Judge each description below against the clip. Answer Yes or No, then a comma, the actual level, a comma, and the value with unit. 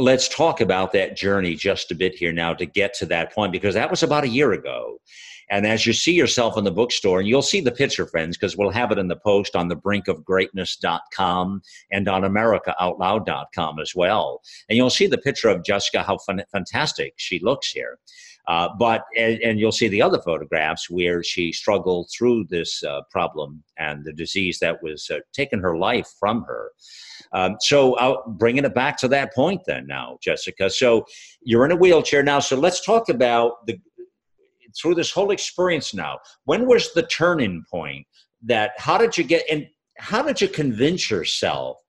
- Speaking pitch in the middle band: No, low, 115 Hz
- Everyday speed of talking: Yes, average, 195 wpm